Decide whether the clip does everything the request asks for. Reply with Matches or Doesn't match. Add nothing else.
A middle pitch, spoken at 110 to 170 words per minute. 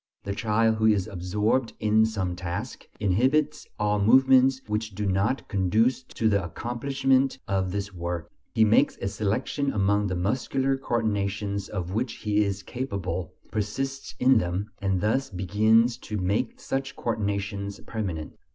Doesn't match